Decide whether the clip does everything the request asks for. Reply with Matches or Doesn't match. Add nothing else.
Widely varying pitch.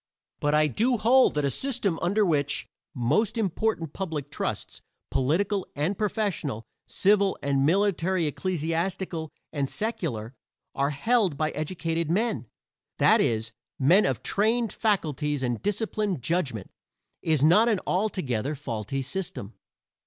Matches